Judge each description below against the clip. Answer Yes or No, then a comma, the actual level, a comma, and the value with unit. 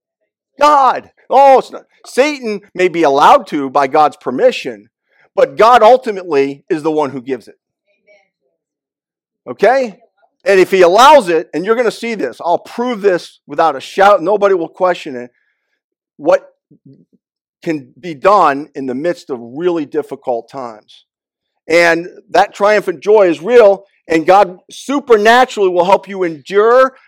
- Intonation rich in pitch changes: Yes, wide, 7.5 semitones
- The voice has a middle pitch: No, high, 195 Hz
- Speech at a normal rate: Yes, average, 150 wpm